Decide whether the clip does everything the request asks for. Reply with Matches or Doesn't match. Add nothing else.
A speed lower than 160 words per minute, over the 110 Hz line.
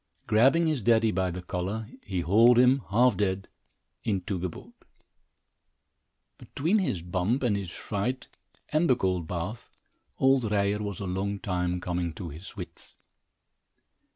Doesn't match